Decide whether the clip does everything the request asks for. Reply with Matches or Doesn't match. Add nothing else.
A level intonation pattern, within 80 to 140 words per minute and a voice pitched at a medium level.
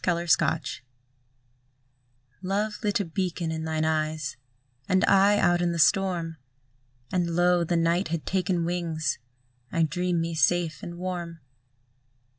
Matches